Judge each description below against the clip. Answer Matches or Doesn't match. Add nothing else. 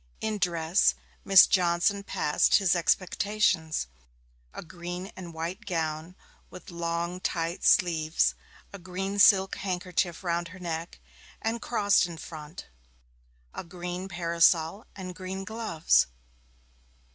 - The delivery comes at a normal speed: Doesn't match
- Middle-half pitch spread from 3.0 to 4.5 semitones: Doesn't match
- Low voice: Doesn't match